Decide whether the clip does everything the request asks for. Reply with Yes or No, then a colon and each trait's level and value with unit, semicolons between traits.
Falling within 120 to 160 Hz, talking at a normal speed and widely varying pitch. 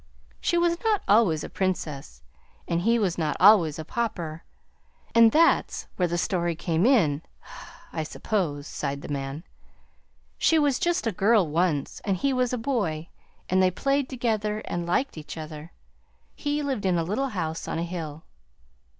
No: medium, 185 Hz; average, 165 wpm; wide, 6.7 semitones